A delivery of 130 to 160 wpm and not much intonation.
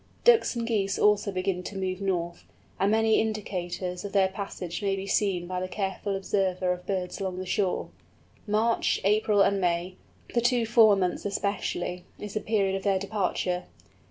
No: average, 175 wpm; narrow, 2.3 semitones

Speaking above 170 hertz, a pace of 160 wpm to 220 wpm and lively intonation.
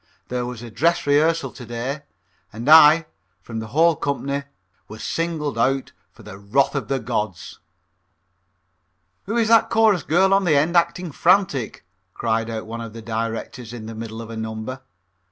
No: low, 135 Hz; average, 170 wpm; wide, 6.5 semitones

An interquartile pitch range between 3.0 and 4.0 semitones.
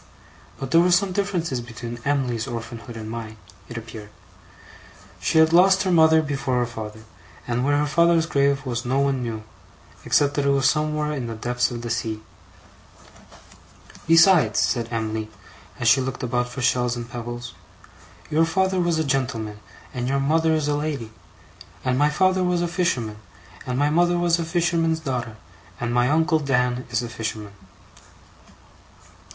No: average, 5.2 semitones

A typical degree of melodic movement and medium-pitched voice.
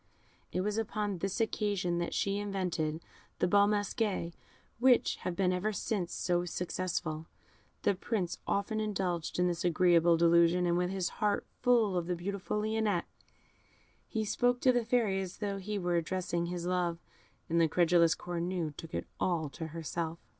Yes: average, 3.2 semitones; medium, 180 Hz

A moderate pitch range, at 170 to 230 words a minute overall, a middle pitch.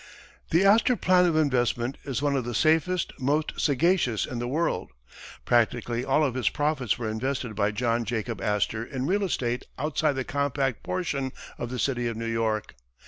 No: average, 4.6 semitones; average, 180 wpm; low, 130 Hz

